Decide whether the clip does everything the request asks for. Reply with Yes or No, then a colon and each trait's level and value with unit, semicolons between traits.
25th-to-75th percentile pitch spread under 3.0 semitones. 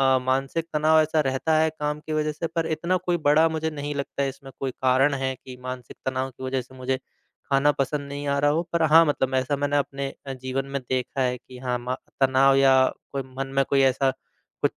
Yes: narrow, 2.4 semitones